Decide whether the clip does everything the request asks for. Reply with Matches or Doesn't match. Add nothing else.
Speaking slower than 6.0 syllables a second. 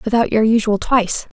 Matches